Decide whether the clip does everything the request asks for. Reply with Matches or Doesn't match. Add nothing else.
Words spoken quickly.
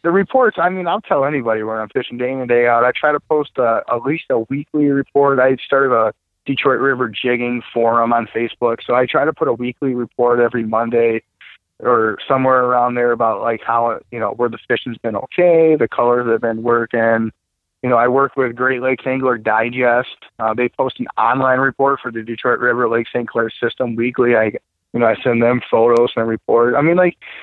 Matches